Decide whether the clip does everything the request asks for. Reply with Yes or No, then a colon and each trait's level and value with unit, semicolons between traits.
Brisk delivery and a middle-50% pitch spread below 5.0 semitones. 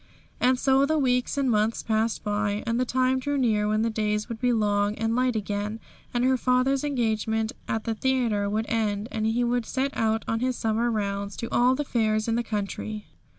Yes: fast, 210 wpm; average, 2.8 semitones